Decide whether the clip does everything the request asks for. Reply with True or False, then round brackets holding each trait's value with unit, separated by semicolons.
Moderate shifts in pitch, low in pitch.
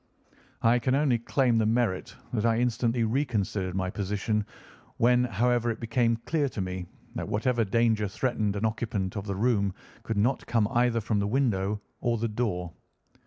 True (3.0 semitones; 115 Hz)